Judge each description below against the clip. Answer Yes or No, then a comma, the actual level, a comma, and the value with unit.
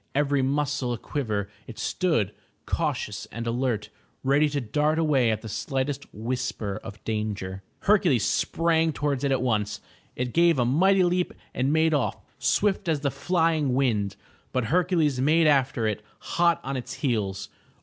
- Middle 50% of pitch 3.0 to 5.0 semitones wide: No, wide, 5.4 semitones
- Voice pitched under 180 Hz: Yes, low, 135 Hz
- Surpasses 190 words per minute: No, average, 160 wpm